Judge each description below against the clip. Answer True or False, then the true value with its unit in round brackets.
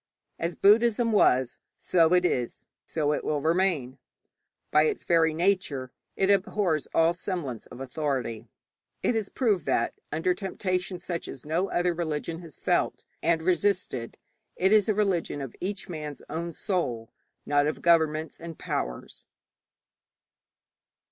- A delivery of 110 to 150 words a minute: True (140 wpm)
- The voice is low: False (165 Hz)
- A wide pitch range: False (3.9 semitones)